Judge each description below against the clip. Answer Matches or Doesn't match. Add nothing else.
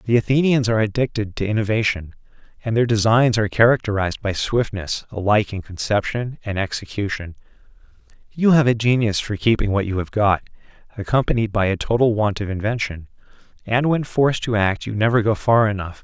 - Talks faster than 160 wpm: Matches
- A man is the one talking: Matches